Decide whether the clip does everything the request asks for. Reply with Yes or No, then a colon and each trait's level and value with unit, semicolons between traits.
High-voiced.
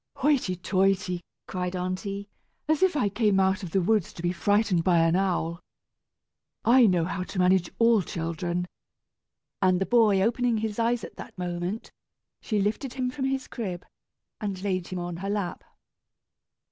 Yes: high, 195 Hz